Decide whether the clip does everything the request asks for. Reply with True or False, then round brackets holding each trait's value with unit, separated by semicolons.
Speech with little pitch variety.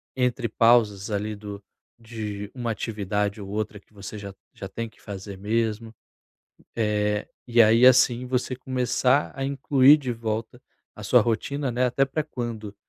False (3.3 semitones)